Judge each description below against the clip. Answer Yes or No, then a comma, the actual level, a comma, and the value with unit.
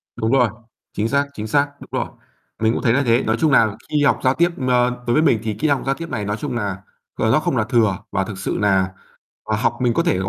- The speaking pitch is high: No, low, 120 Hz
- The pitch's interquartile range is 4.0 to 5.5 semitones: Yes, average, 4.6 semitones